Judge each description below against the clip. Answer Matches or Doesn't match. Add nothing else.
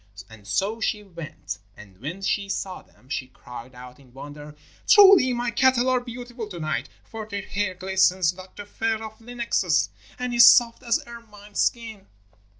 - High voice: Matches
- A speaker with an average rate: Matches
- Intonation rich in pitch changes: Matches